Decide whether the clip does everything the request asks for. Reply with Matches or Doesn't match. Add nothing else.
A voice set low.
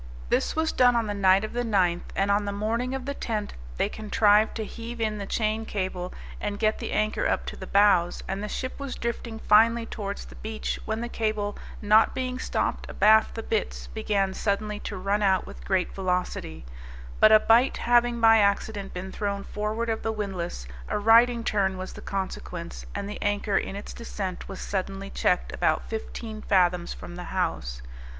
Doesn't match